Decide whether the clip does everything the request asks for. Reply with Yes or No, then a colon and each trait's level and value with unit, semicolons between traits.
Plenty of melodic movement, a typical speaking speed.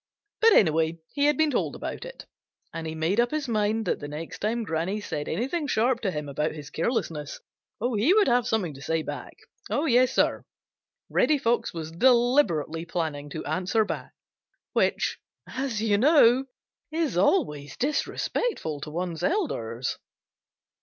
Yes: wide, 8.4 semitones; average, 155 wpm